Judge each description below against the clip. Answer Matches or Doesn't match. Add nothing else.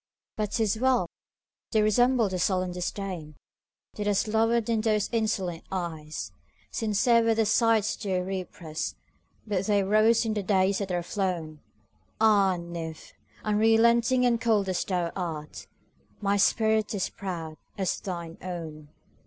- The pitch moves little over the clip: Doesn't match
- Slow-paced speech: Matches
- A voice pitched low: Doesn't match